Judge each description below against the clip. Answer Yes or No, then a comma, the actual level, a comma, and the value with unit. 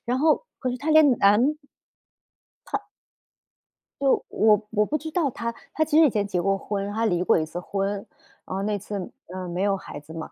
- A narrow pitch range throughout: No, wide, 5.4 semitones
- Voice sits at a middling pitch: No, high, 210 Hz